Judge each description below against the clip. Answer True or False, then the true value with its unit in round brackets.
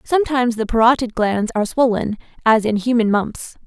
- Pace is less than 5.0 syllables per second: False (5.7 syllables/s)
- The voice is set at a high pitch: True (230 Hz)